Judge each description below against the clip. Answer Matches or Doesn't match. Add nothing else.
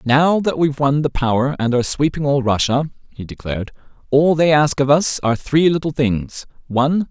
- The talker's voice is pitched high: Doesn't match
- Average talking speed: Matches